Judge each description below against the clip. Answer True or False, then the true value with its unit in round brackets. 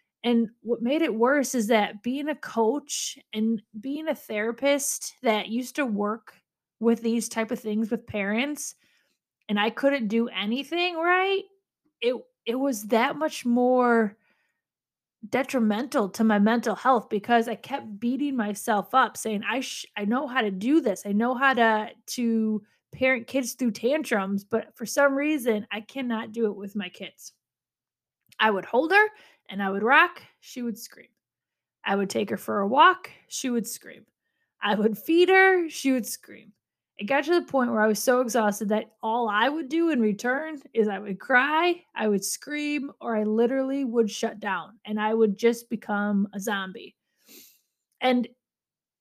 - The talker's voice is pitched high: True (235 Hz)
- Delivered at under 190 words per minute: True (175 wpm)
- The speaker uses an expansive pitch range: False (4.3 semitones)